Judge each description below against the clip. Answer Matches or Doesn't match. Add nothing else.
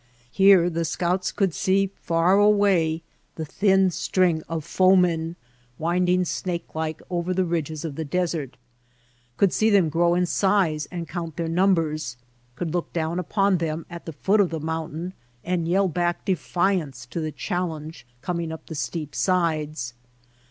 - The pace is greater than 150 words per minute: Matches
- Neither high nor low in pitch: Matches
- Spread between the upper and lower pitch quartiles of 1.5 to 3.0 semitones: Matches